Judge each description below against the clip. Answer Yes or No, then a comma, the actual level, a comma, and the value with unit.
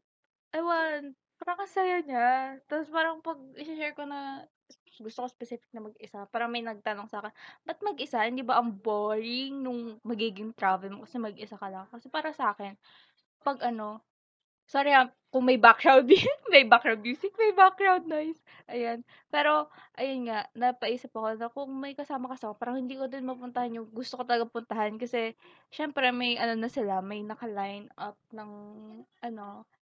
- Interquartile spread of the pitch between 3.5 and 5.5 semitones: Yes, average, 4.3 semitones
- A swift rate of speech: Yes, fast, 170 wpm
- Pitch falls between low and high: No, high, 245 Hz